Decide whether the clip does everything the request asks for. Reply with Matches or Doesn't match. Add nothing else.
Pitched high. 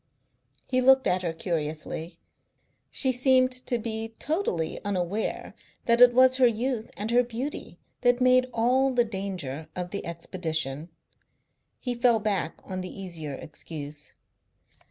Matches